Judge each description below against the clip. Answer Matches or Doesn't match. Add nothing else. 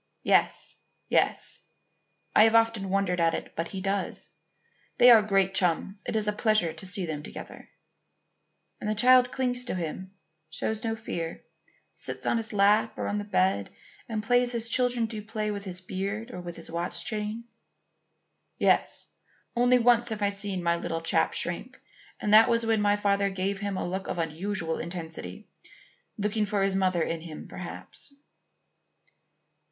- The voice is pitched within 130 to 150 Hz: Doesn't match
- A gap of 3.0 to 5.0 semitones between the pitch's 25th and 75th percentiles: Matches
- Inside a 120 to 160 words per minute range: Doesn't match